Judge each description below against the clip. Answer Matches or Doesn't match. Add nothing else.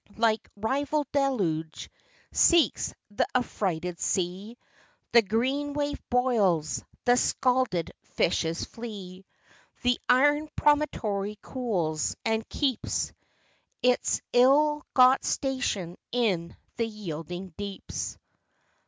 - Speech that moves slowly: Matches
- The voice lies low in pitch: Doesn't match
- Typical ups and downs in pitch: Doesn't match